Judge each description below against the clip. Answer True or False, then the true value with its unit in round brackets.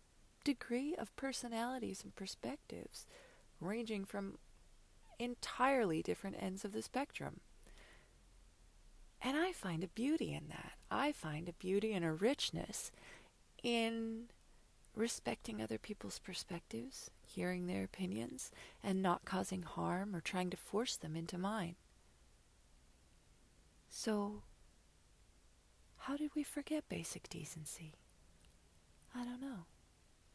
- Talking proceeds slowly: True (110 wpm)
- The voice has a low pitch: False (195 Hz)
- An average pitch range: False (7.0 semitones)